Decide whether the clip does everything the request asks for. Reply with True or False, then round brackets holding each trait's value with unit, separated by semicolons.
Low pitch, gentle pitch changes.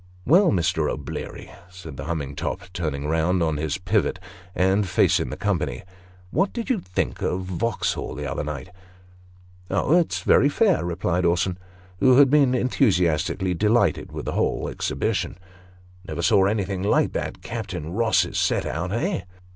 False (90 Hz; 4.2 semitones)